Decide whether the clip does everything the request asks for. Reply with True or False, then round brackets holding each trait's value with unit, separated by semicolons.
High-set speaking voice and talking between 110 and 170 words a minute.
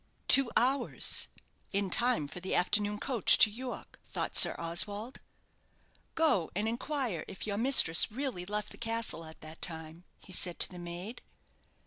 True (205 Hz; 155 wpm)